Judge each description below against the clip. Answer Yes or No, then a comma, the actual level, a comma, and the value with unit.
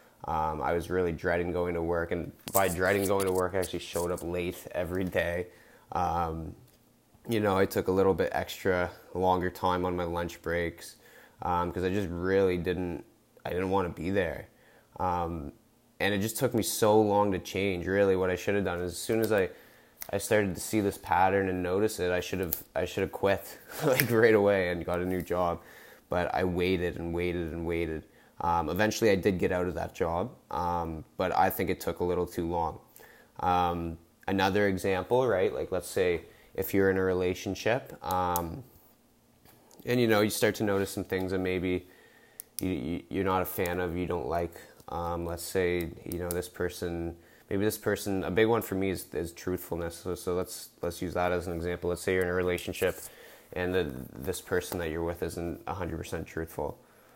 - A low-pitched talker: Yes, very low, 90 Hz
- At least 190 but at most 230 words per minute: Yes, fast, 205 wpm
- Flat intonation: Yes, narrow, 1.8 semitones